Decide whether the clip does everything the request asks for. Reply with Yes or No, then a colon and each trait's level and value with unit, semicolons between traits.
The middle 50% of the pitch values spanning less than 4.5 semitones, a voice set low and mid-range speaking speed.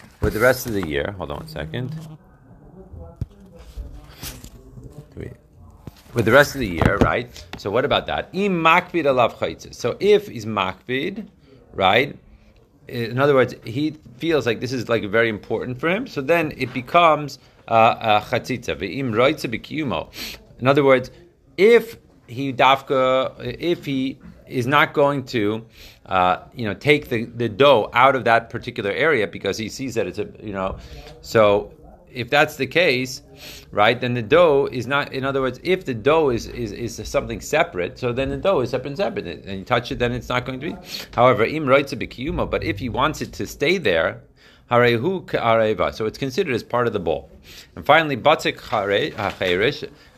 No: average, 3.9 semitones; low, 130 Hz; fast, 165 wpm